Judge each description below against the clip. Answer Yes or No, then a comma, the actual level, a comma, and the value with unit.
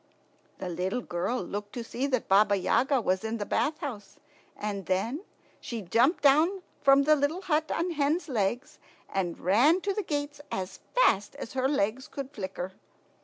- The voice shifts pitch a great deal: Yes, wide, 6.6 semitones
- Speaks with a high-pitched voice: Yes, very high, 250 Hz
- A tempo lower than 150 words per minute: No, average, 170 wpm